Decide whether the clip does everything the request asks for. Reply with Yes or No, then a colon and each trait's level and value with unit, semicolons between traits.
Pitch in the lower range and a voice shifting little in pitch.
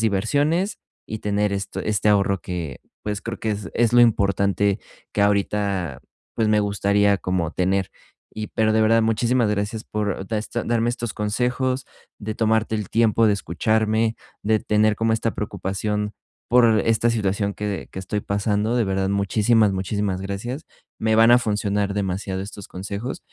Yes: low, 105 Hz; narrow, 2.0 semitones